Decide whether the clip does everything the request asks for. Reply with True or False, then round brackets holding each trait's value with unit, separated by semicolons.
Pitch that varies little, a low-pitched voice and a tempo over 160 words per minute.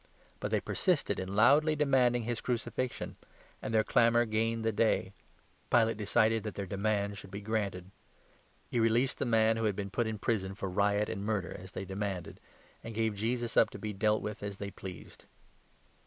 True (2.3 semitones; 110 Hz; 185 wpm)